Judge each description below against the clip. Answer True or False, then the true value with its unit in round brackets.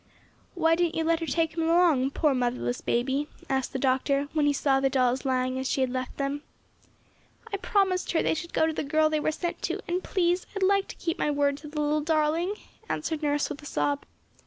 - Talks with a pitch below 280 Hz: False (300 Hz)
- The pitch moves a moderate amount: True (3.5 semitones)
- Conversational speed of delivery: False (230 wpm)